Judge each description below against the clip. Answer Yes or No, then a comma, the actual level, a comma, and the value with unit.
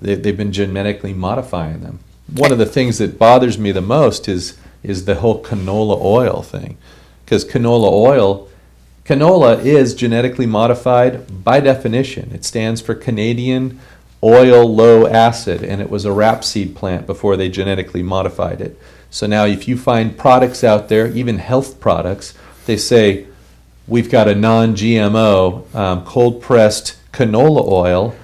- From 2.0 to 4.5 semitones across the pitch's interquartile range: Yes, average, 3.7 semitones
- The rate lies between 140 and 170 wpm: Yes, average, 155 wpm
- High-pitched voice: No, low, 110 Hz